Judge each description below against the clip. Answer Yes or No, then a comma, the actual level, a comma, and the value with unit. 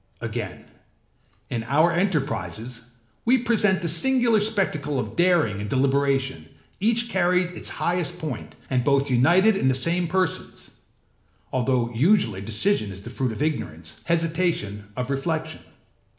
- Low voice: No, medium, 155 Hz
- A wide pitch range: Yes, wide, 6.5 semitones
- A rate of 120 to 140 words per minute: Yes, slow, 135 wpm